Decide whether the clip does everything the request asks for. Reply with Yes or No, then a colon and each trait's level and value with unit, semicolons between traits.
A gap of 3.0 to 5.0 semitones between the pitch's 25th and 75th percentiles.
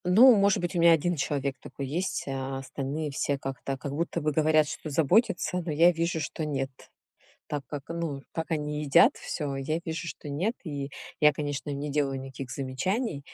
Yes: average, 3.4 semitones